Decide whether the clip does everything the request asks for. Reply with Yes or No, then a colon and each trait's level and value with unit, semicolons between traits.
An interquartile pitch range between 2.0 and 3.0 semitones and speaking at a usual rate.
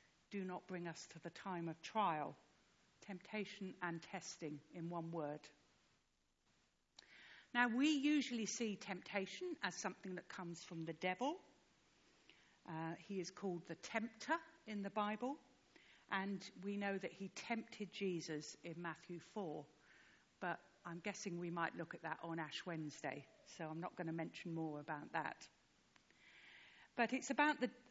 No: average, 4.2 semitones; average, 150 wpm